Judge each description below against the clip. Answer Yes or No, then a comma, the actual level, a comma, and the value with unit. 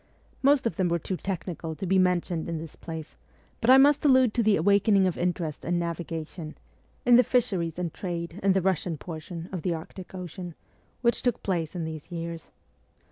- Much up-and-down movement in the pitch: No, average, 3.2 semitones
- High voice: No, medium, 180 Hz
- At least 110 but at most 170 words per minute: No, average, 190 wpm